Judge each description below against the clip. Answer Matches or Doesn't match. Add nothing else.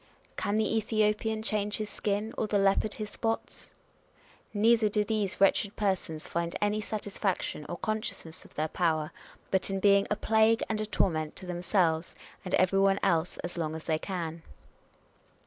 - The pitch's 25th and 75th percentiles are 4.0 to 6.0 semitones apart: Doesn't match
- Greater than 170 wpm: Matches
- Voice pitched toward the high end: Matches